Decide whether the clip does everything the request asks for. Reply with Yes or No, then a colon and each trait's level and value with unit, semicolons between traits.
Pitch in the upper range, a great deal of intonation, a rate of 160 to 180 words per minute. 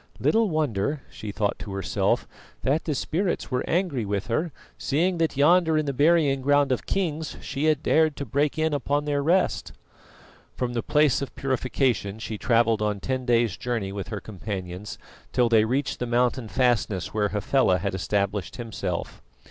No: low, 130 Hz; wide, 5.9 semitones; average, 170 wpm